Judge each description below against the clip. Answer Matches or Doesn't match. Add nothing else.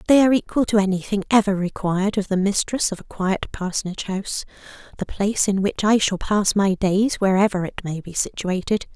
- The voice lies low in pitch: Doesn't match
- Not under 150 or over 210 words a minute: Matches